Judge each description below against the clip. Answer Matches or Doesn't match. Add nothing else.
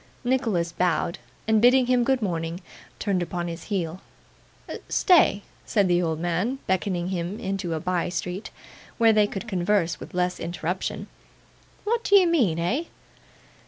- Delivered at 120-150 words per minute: Matches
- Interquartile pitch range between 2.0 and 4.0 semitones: Doesn't match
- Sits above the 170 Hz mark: Matches